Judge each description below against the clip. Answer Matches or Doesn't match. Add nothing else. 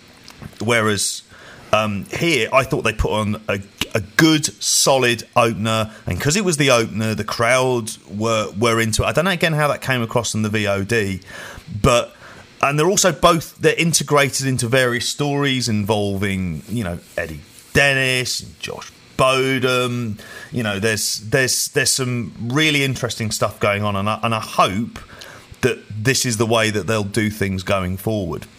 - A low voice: Matches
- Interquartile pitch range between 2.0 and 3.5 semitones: Doesn't match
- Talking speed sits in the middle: Matches